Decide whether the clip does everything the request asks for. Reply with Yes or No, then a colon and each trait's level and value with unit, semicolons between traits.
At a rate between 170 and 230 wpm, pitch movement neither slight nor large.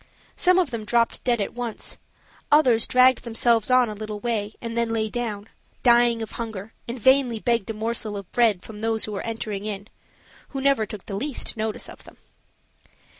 No: average, 190 wpm; narrow, 2.2 semitones